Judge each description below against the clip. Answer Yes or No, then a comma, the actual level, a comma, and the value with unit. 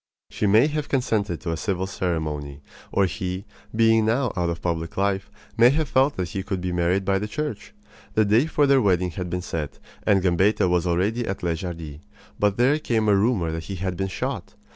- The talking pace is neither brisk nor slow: No, fast, 210 wpm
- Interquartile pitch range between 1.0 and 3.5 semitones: No, average, 4.2 semitones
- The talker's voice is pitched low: Yes, very low, 95 Hz